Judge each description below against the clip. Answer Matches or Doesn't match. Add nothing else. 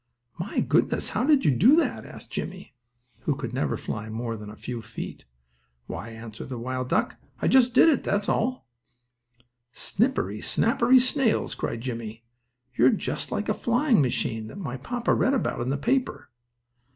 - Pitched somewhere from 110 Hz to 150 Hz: Matches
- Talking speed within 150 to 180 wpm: Matches